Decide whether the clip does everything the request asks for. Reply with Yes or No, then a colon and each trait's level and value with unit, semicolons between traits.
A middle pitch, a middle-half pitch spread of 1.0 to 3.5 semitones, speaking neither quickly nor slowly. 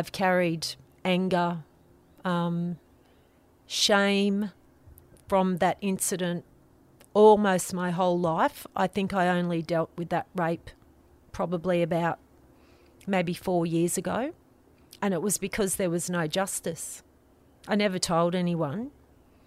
No: medium, 175 Hz; average, 2.7 semitones; slow, 115 wpm